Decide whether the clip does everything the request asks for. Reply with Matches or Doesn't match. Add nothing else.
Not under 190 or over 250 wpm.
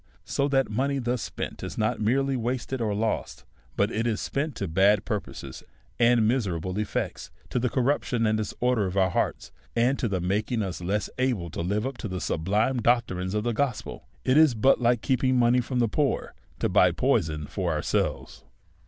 Matches